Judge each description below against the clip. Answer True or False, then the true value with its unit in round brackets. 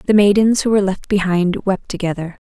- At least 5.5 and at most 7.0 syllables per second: True (5.8 syllables/s)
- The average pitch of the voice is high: True (195 Hz)